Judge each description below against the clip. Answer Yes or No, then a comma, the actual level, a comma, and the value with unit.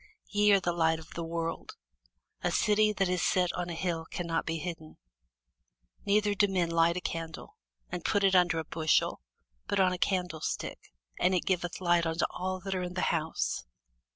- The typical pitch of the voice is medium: Yes, medium, 175 Hz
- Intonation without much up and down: Yes, narrow, 2.3 semitones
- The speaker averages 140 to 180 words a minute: No, average, 190 wpm